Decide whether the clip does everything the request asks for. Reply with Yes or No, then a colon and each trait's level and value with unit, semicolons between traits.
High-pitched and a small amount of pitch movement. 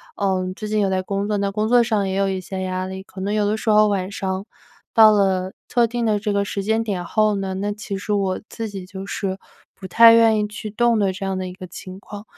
Yes: high, 200 Hz; narrow, 2.1 semitones